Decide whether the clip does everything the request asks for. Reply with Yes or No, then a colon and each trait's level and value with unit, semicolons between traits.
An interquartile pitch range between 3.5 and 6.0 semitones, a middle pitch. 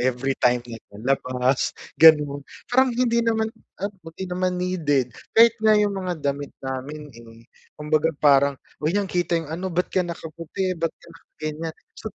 Yes: average, 5.2 semitones; medium, 160 Hz